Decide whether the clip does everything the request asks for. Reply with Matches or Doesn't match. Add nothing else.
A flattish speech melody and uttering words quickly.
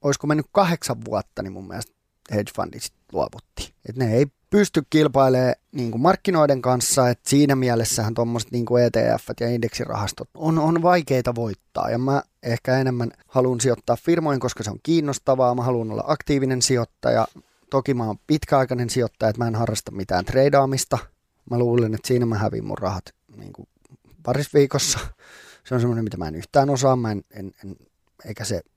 Doesn't match